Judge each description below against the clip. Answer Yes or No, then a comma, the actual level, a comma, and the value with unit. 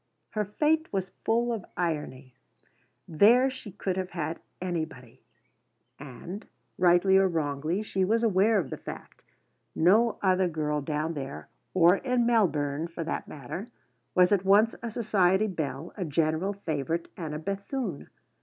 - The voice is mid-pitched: Yes, medium, 180 Hz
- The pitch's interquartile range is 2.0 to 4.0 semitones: No, average, 4.8 semitones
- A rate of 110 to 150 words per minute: Yes, average, 145 wpm